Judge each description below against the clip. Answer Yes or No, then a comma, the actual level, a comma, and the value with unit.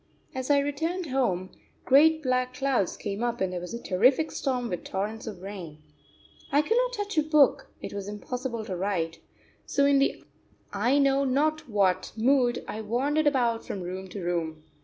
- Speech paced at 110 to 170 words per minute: No, average, 180 wpm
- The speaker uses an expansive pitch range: Yes, wide, 6.4 semitones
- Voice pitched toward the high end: Yes, high, 245 Hz